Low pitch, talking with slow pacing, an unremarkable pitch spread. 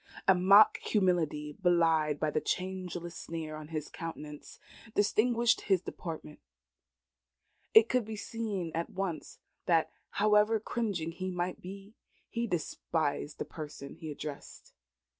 No: medium, 175 Hz; slow, 125 wpm; average, 4.5 semitones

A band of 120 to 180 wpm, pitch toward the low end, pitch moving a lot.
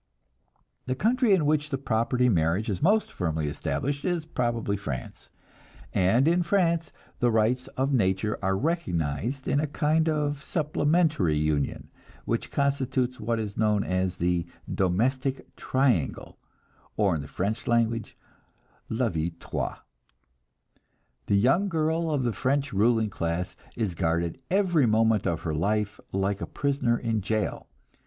Yes: average, 140 wpm; low, 115 Hz; wide, 7.1 semitones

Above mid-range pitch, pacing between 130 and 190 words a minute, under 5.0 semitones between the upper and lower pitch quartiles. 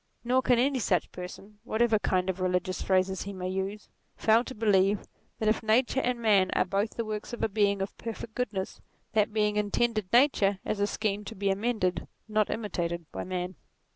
No: high, 210 Hz; average, 200 wpm; average, 3.0 semitones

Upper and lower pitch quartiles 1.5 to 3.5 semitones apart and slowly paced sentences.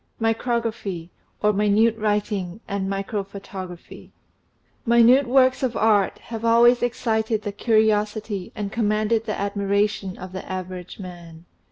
Yes: narrow, 2.6 semitones; slow, 120 wpm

